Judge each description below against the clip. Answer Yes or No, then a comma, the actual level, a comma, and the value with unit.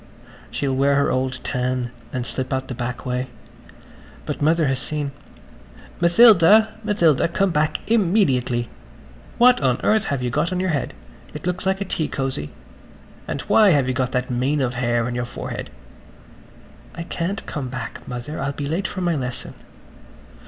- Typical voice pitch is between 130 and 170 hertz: Yes, medium, 140 Hz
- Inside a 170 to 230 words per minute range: Yes, average, 175 wpm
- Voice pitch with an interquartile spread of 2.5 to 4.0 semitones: No, average, 5.3 semitones